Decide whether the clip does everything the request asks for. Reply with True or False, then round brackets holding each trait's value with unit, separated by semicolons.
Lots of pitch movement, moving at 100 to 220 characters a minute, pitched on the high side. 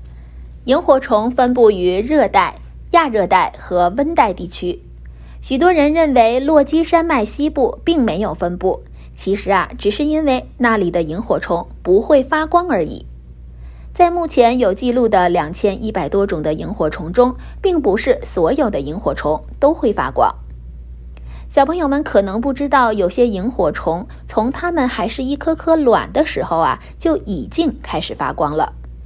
False (8.8 semitones; 240 characters per minute; 230 Hz)